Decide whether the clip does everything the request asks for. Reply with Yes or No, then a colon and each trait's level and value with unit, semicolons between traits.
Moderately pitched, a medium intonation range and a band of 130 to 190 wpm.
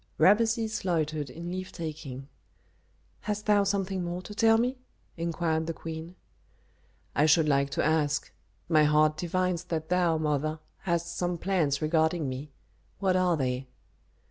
Yes: medium, 165 Hz; average, 3.2 semitones; average, 145 wpm